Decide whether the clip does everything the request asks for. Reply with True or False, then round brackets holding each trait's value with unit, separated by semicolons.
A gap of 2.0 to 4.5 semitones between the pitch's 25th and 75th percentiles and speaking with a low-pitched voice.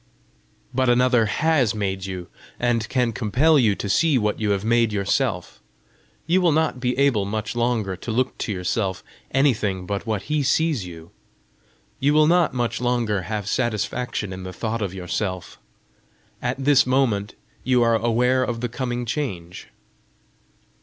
True (4.1 semitones; 115 Hz)